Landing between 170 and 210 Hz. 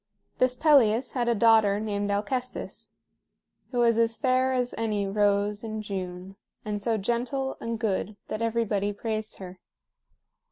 No: high, 220 Hz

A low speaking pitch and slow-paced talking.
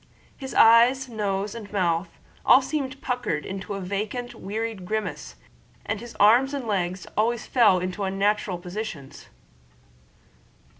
No: high, 210 Hz; slow, 130 wpm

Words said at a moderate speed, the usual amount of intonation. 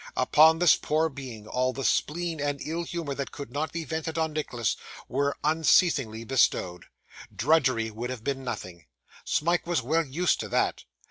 Yes: average, 170 wpm; average, 4.2 semitones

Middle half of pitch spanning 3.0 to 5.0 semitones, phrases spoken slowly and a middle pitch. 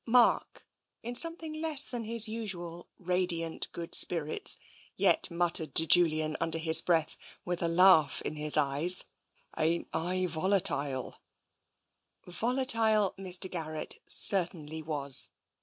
Yes: average, 3.7 semitones; slow, 125 wpm; medium, 175 Hz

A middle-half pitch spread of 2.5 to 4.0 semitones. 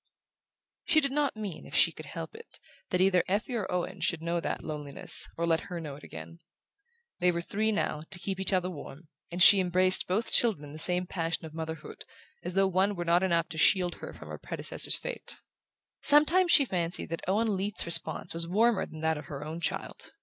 Yes: average, 3.3 semitones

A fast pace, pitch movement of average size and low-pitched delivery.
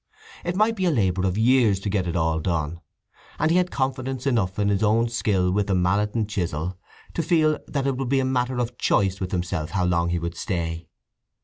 No: fast, 225 wpm; wide, 6.5 semitones; low, 105 Hz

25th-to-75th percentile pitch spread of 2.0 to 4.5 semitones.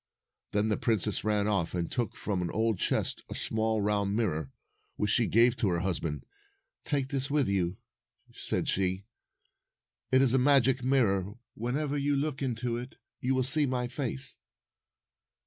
No: average, 4.9 semitones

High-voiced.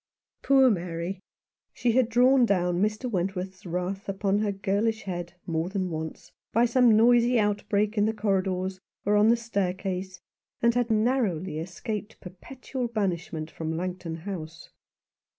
Yes: high, 195 Hz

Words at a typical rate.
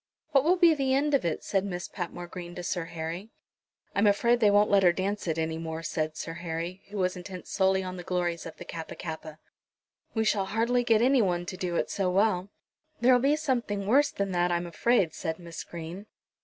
No: fast, 225 wpm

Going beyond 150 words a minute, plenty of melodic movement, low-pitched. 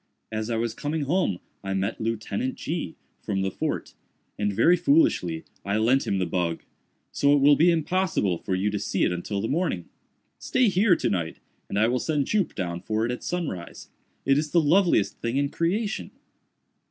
Yes: average, 190 wpm; wide, 9.0 semitones; low, 115 Hz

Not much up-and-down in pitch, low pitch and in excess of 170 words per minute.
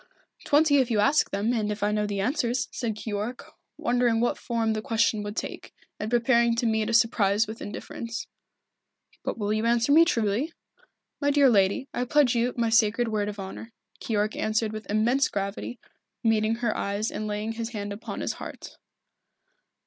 No: narrow, 2.3 semitones; high, 225 Hz; average, 180 wpm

